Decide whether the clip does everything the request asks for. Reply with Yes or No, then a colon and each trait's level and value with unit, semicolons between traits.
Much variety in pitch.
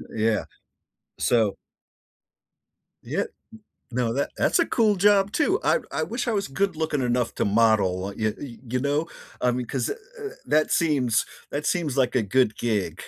Yes: wide, 7.7 semitones